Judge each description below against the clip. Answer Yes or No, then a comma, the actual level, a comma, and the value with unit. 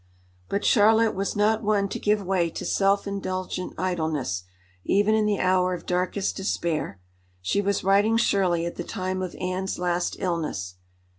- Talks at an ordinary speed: Yes, average, 160 wpm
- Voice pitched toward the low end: No, medium, 185 Hz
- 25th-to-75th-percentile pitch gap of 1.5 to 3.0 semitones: Yes, narrow, 2.4 semitones